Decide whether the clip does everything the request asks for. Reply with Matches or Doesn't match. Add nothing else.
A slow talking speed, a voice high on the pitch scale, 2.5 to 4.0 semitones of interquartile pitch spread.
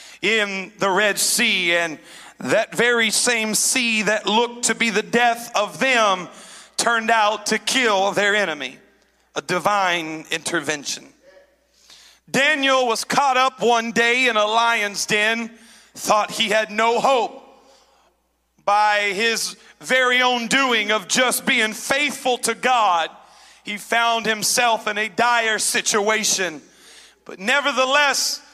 Matches